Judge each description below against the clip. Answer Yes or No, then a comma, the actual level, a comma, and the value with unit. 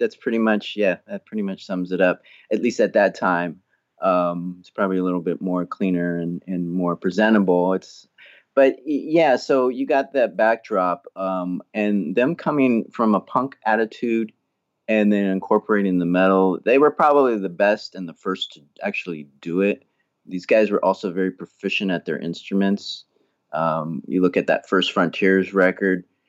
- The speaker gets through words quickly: No, average, 175 wpm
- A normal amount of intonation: Yes, average, 3.6 semitones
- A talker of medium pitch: No, very low, 95 Hz